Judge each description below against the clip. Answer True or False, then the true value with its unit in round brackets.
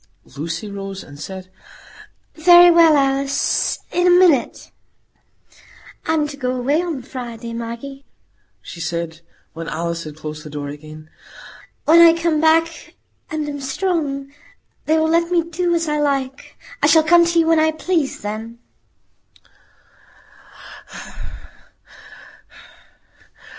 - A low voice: False (280 Hz)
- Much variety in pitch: True (8.5 semitones)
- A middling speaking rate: False (125 wpm)